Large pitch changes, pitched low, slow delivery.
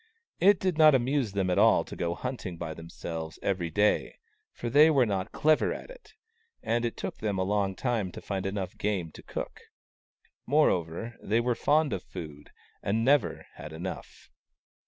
No: wide, 6.4 semitones; low, 105 Hz; average, 175 wpm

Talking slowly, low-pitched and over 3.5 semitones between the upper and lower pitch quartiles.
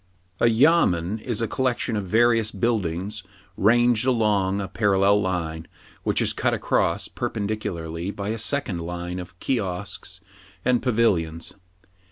Yes: slow, 130 wpm; low, 100 Hz; average, 4.5 semitones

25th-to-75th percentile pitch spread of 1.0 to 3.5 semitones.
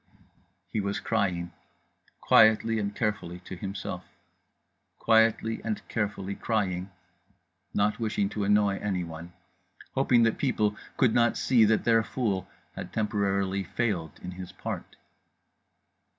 Yes: average, 2.7 semitones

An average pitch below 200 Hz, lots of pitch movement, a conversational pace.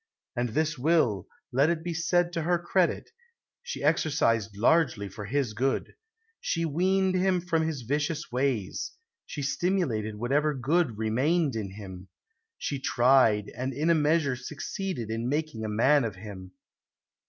Yes: medium, 140 Hz; wide, 6.7 semitones; average, 150 wpm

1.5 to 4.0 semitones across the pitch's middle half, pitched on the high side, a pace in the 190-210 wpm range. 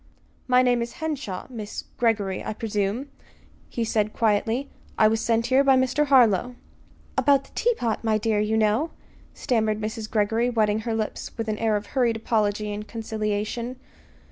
No: narrow, 2.6 semitones; high, 225 Hz; average, 165 wpm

